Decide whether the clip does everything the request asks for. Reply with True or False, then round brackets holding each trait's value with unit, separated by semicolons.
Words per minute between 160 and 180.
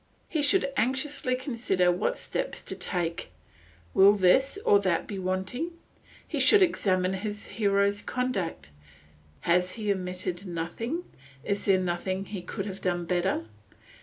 False (135 wpm)